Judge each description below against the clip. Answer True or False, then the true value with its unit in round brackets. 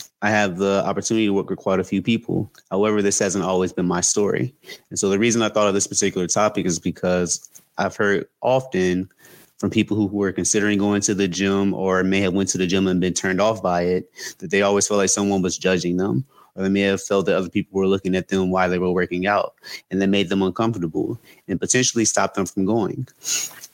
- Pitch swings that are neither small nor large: False (1.7 semitones)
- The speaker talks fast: True (235 wpm)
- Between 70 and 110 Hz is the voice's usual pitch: True (95 Hz)